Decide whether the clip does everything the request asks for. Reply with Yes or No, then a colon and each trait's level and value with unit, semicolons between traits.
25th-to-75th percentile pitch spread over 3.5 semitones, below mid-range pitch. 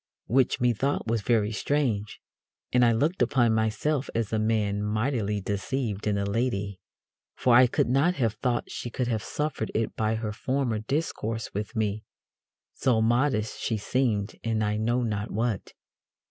No: average, 2.9 semitones; low, 115 Hz